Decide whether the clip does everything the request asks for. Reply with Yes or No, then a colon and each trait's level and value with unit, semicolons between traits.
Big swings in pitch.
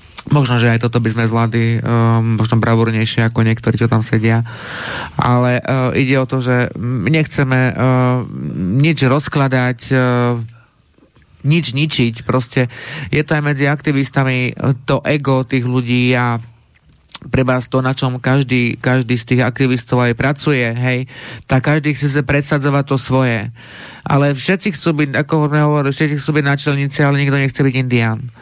No: average, 2.9 semitones